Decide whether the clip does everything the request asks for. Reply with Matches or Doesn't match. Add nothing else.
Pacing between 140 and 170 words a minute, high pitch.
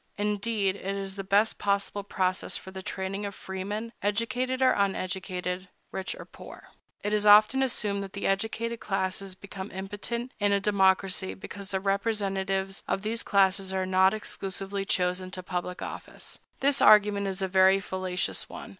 Matches